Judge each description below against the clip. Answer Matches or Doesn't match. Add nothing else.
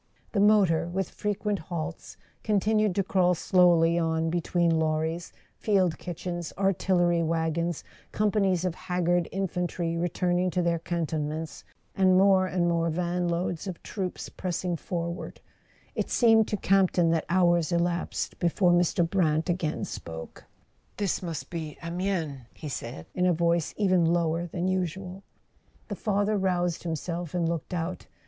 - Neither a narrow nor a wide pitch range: Doesn't match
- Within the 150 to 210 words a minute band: Doesn't match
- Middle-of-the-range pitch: Matches